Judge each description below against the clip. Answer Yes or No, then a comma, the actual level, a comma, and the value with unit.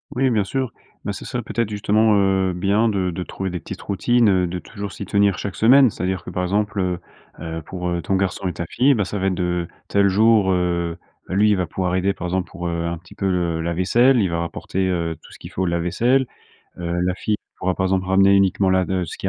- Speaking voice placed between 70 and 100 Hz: Yes, very low, 95 Hz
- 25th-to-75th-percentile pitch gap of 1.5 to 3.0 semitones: Yes, narrow, 2.5 semitones